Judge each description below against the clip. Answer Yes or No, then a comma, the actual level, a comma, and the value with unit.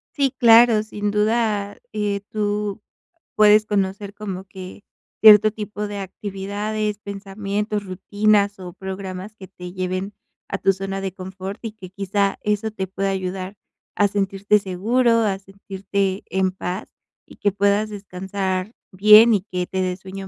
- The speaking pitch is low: No, high, 200 Hz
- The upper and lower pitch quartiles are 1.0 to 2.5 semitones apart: Yes, narrow, 1.7 semitones